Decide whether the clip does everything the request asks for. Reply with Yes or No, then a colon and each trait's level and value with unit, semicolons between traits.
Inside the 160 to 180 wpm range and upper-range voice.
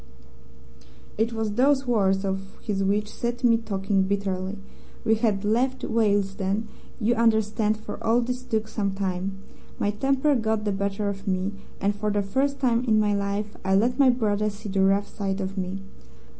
Yes: average, 175 wpm; high, 210 Hz